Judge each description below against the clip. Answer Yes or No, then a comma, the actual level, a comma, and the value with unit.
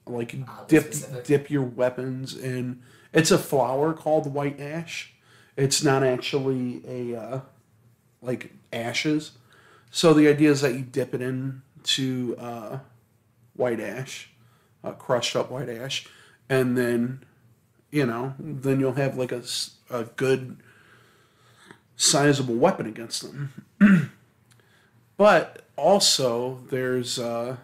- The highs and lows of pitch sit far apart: No, average, 3.0 semitones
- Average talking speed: No, slow, 120 wpm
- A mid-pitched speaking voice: No, low, 130 Hz